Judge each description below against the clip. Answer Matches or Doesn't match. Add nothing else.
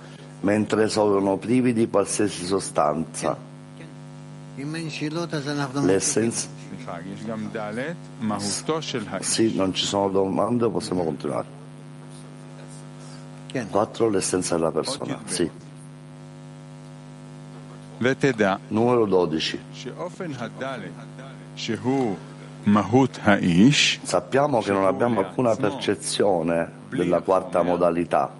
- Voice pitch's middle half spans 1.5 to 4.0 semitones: Doesn't match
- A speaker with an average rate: Doesn't match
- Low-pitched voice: Matches